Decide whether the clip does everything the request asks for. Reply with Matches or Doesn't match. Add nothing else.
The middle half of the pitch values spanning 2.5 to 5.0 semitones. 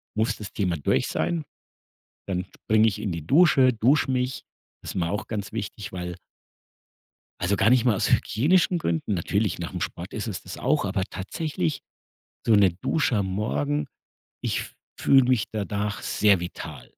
Doesn't match